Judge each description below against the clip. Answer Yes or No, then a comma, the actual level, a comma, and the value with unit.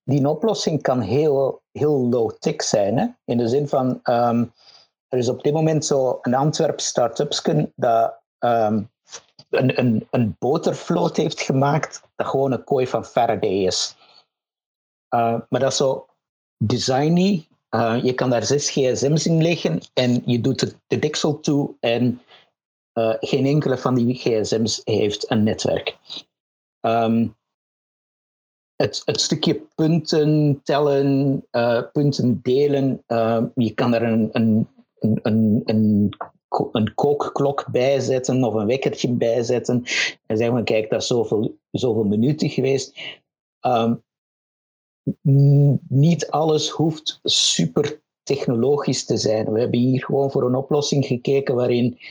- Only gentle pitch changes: No, average, 3.5 semitones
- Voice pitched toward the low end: Yes, low, 130 Hz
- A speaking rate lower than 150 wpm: Yes, average, 140 wpm